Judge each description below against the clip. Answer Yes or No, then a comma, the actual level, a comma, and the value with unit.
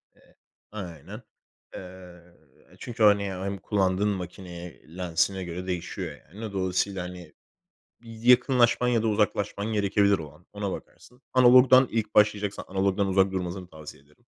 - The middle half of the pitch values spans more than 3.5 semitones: No, average, 2.9 semitones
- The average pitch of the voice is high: No, low, 100 Hz